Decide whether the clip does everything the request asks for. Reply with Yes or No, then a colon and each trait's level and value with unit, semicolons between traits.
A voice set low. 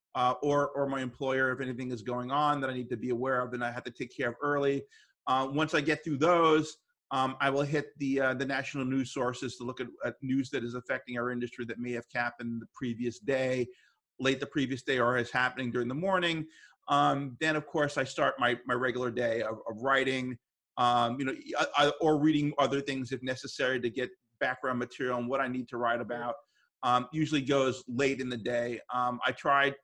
Yes: low, 130 Hz